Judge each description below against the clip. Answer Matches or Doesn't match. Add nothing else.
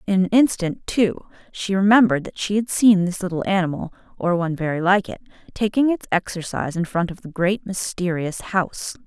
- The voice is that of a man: Doesn't match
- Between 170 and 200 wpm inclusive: Matches